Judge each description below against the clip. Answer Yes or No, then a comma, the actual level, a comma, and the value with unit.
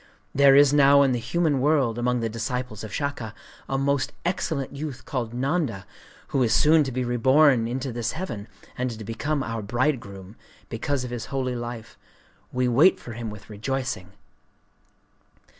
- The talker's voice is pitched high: No, low, 125 Hz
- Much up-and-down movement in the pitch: No, average, 3.5 semitones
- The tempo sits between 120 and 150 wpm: No, average, 165 wpm